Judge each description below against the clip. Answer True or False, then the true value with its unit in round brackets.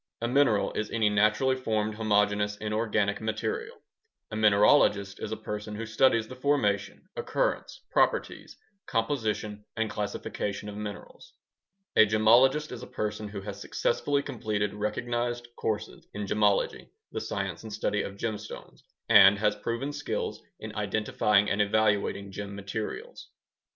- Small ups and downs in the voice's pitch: True (2.1 semitones)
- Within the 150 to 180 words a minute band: False (135 wpm)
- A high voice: False (105 Hz)